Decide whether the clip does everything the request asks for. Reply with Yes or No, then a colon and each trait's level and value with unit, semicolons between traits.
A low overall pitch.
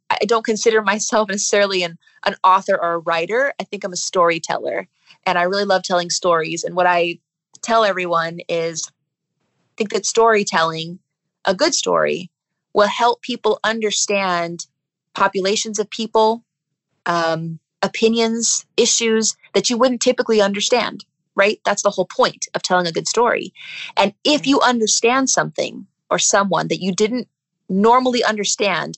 No: high, 195 Hz